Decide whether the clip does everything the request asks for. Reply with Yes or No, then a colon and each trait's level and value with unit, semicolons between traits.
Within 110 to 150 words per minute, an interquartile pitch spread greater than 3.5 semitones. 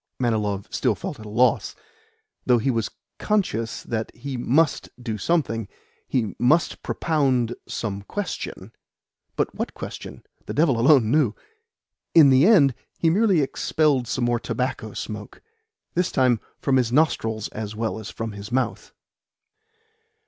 Yes: average, 140 wpm; average, 5.0 semitones